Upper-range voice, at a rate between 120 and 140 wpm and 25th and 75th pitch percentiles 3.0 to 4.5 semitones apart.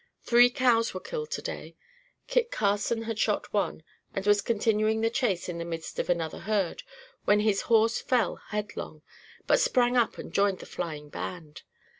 No: high, 210 Hz; average, 170 wpm; average, 4.2 semitones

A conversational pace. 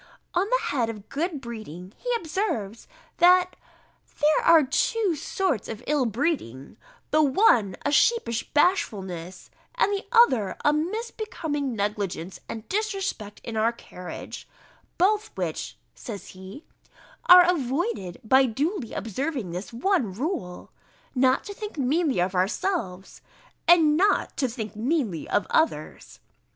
No: slow, 130 wpm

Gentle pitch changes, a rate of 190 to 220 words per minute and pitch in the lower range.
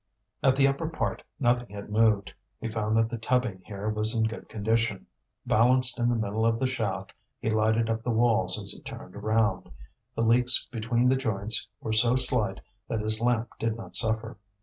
Yes: narrow, 1.9 semitones; average, 195 wpm; low, 115 Hz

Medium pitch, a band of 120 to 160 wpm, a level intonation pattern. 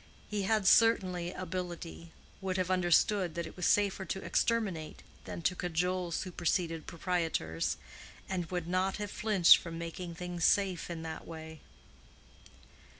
Yes: medium, 180 Hz; average, 140 wpm; narrow, 2.1 semitones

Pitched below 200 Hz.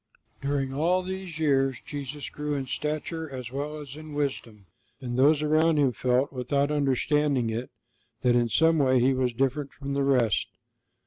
Yes: medium, 140 Hz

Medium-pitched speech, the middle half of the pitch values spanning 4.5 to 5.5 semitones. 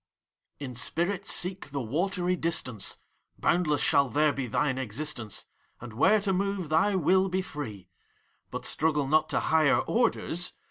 Yes: medium, 155 Hz; average, 5.0 semitones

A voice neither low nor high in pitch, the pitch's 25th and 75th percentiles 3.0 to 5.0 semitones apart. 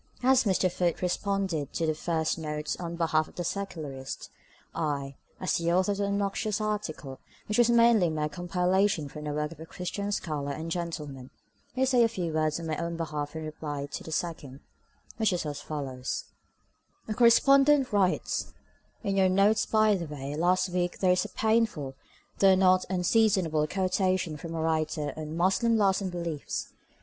Yes: medium, 175 Hz; average, 4.4 semitones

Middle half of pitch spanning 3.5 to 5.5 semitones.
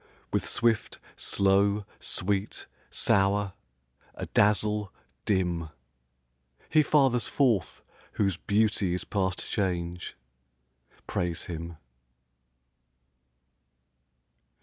No: average, 2.8 semitones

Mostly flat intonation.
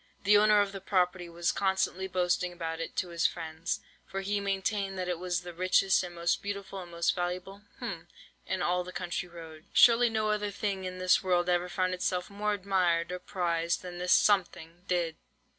Yes: narrow, 2.0 semitones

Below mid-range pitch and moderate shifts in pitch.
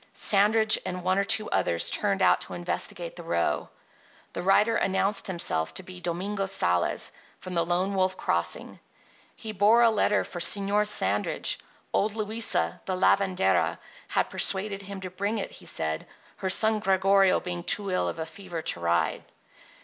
No: high, 190 Hz; average, 3.3 semitones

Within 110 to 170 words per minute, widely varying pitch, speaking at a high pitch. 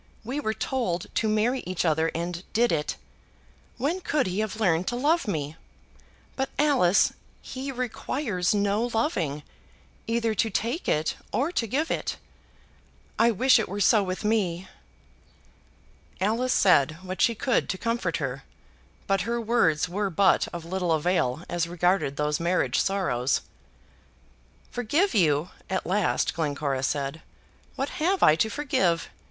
Yes: average, 145 wpm; wide, 6.0 semitones; high, 195 Hz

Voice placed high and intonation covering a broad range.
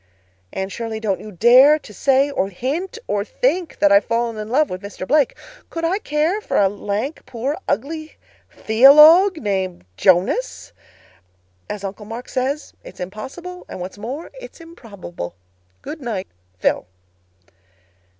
Yes: high, 245 Hz; wide, 7.2 semitones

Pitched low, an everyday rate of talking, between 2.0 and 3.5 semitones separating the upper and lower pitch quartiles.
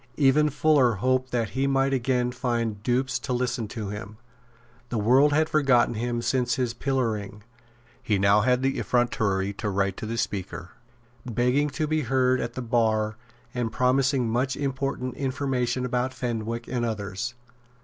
Yes: low, 125 Hz; average, 160 wpm; average, 2.8 semitones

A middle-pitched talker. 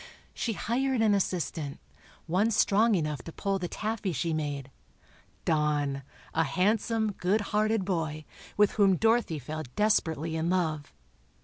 Yes: medium, 180 Hz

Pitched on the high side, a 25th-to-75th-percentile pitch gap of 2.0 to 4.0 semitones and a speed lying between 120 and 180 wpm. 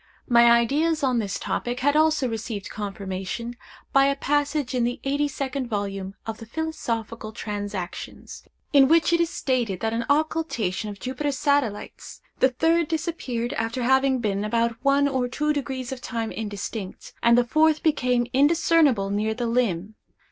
No: high, 245 Hz; average, 4.4 semitones; average, 160 wpm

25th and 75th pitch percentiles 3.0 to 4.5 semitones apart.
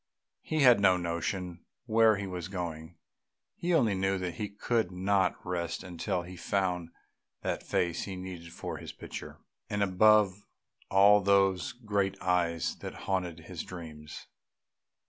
No: narrow, 2.5 semitones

